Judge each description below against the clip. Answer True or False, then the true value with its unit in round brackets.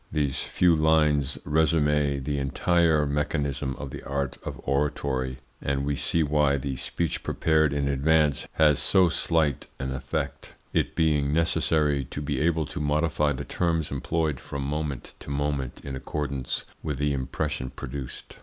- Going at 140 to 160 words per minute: True (155 wpm)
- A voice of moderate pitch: False (75 Hz)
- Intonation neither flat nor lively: False (2.0 semitones)